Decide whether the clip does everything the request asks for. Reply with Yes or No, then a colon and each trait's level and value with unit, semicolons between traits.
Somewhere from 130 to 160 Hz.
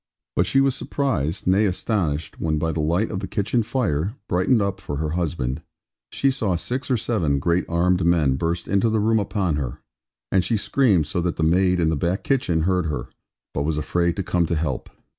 No: very low, 90 Hz